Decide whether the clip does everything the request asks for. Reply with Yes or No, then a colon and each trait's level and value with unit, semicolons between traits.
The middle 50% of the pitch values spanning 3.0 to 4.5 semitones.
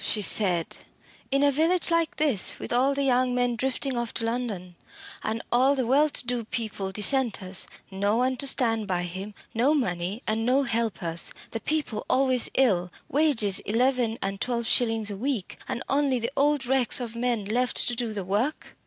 Yes: average, 4.1 semitones